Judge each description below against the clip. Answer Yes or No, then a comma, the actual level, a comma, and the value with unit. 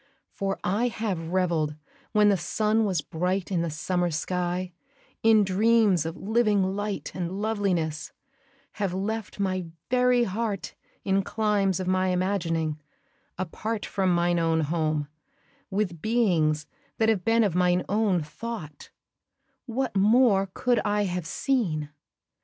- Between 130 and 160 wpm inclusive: Yes, slow, 135 wpm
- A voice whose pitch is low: No, high, 190 Hz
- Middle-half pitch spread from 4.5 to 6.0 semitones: No, average, 3.7 semitones